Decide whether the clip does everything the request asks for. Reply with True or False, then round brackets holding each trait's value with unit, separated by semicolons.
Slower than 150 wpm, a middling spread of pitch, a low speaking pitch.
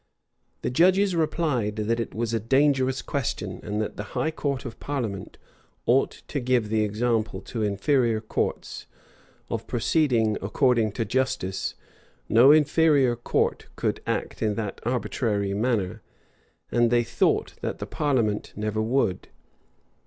True (140 wpm; 4.0 semitones; 120 Hz)